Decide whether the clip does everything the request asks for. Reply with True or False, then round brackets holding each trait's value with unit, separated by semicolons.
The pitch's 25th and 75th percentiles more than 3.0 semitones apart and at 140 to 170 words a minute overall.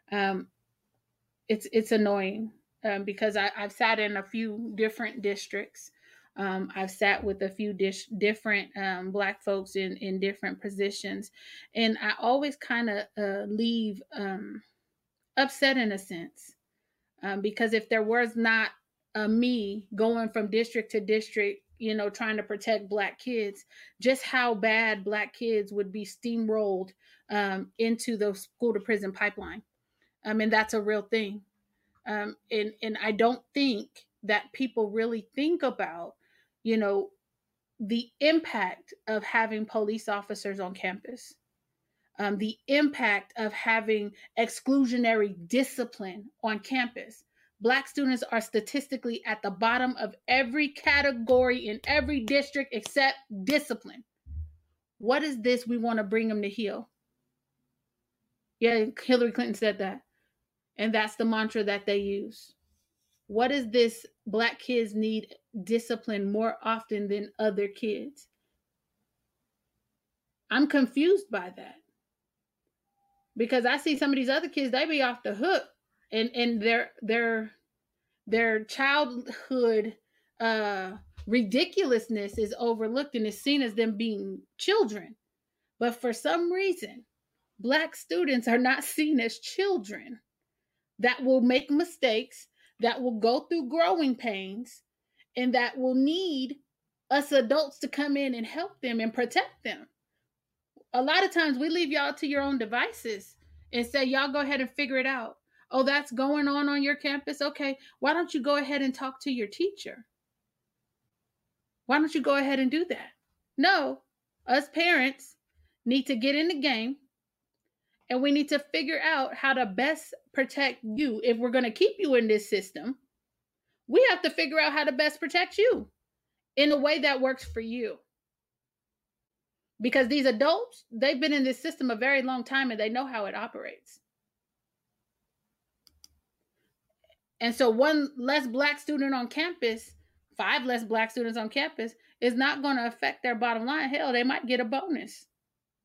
True (4.5 semitones; 150 wpm)